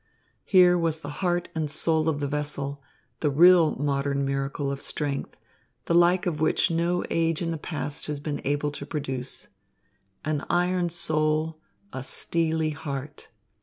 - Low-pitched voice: No, medium, 155 Hz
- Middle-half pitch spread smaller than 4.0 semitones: Yes, average, 2.7 semitones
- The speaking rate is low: No, average, 155 wpm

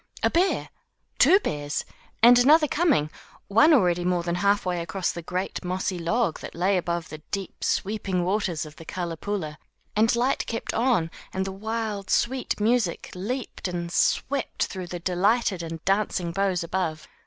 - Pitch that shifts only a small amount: No, average, 4.6 semitones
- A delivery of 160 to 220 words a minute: Yes, average, 165 wpm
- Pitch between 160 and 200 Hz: Yes, high, 190 Hz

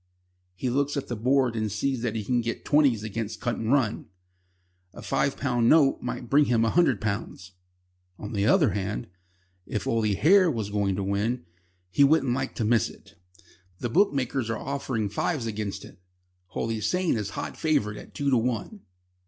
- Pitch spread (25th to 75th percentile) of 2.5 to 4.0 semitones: No, average, 4.5 semitones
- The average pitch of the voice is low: Yes, low, 115 Hz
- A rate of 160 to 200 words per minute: Yes, average, 175 wpm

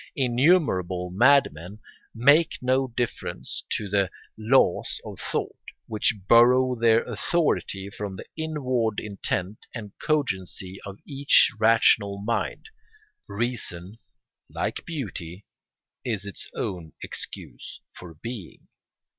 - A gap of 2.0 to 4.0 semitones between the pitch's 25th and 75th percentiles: No, average, 5.0 semitones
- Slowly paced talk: Yes, slow, 105 wpm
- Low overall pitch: Yes, low, 110 Hz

